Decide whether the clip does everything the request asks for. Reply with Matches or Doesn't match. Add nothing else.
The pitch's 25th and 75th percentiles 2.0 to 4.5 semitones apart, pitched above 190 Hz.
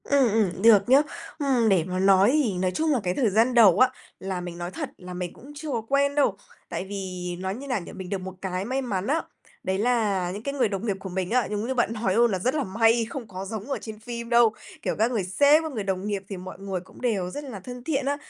Doesn't match